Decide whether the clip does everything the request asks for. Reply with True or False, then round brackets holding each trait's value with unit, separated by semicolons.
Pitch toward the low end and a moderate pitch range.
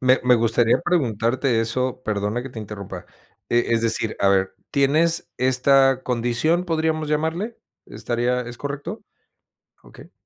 True (125 Hz; 4.2 semitones)